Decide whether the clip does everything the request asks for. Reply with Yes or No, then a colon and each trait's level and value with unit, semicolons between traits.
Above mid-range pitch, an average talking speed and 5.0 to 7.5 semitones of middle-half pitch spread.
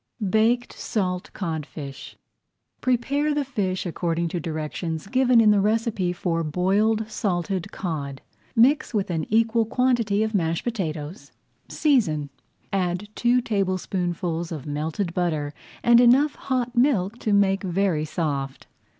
No: high, 195 Hz; slow, 125 wpm; wide, 5.5 semitones